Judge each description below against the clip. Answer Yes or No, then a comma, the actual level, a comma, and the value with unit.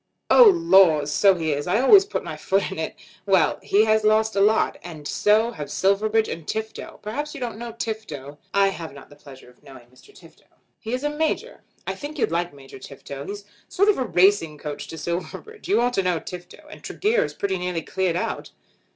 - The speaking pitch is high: Yes, high, 195 Hz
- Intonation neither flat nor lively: No, wide, 5.8 semitones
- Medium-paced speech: No, fast, 215 wpm